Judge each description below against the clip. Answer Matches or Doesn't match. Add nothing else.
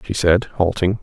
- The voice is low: Matches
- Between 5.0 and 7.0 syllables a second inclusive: Doesn't match